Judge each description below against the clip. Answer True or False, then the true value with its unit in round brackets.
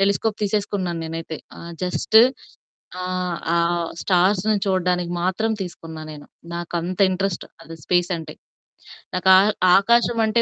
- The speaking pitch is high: False (180 Hz)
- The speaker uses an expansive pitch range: False (2.7 semitones)